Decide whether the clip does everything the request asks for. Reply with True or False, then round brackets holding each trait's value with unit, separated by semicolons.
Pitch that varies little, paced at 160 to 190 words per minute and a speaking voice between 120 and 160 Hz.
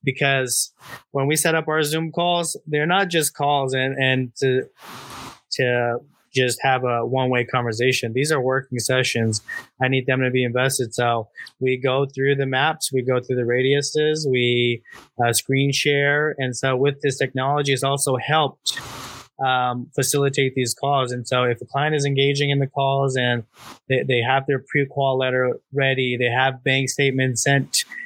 True (1.8 semitones; 175 wpm; 130 Hz)